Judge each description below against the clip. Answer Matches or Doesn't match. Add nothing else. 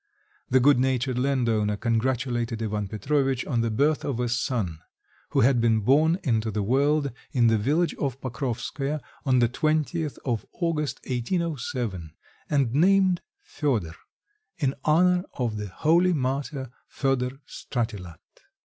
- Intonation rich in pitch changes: Doesn't match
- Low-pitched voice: Matches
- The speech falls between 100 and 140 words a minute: Matches